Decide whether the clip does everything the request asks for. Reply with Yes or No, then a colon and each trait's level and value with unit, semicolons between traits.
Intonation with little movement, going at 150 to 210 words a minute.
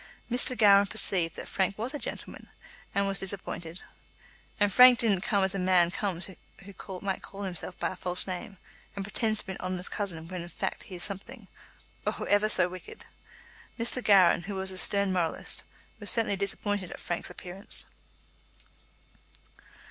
Yes: narrow, 2.0 semitones; average, 170 wpm